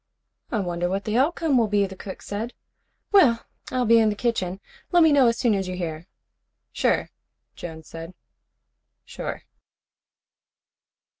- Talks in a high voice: Yes, high, 210 Hz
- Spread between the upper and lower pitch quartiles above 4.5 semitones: Yes, average, 4.9 semitones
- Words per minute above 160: No, average, 150 wpm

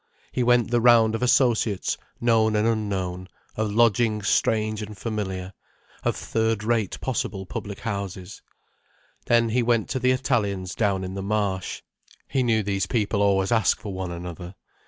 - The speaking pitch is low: Yes, low, 105 Hz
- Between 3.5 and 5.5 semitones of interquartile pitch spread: No, average, 3.1 semitones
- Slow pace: No, average, 155 wpm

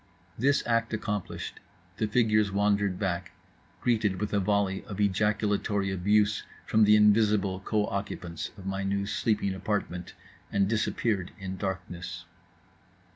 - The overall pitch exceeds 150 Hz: No, low, 100 Hz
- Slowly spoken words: Yes, slow, 130 wpm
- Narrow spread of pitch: Yes, narrow, 1.8 semitones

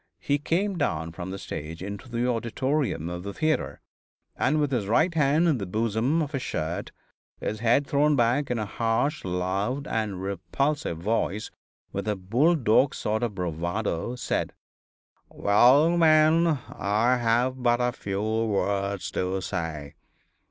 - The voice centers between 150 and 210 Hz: No, low, 115 Hz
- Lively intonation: Yes, wide, 6.3 semitones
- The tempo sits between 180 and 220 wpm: No, average, 150 wpm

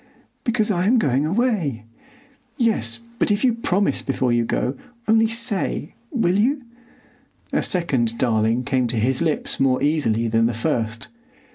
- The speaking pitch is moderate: Yes, medium, 150 Hz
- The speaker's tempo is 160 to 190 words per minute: No, average, 145 wpm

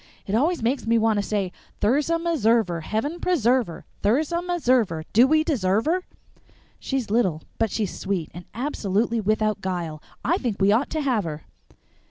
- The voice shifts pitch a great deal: Yes, wide, 6.2 semitones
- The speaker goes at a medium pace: Yes, average, 170 wpm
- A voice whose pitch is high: Yes, high, 225 Hz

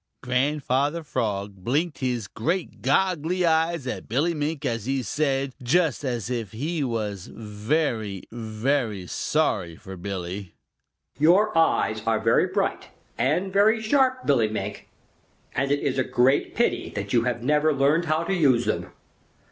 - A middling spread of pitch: No, wide, 6.2 semitones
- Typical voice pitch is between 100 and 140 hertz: Yes, low, 135 Hz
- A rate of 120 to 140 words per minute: No, average, 150 wpm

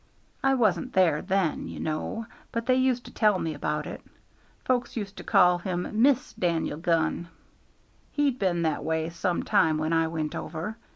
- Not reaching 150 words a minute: No, average, 175 wpm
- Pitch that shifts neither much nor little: No, wide, 5.9 semitones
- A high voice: No, medium, 180 Hz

